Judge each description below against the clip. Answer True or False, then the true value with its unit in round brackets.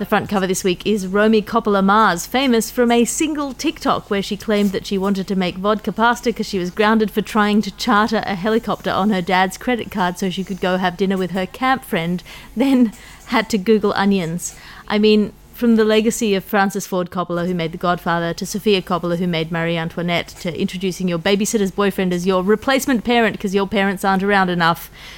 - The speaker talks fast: True (210 wpm)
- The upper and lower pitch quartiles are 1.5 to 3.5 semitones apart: True (2.9 semitones)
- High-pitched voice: True (200 Hz)